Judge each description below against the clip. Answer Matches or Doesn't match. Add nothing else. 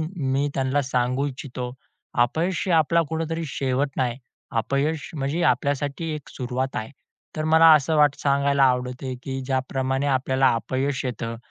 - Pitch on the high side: Doesn't match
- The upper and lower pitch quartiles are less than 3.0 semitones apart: Matches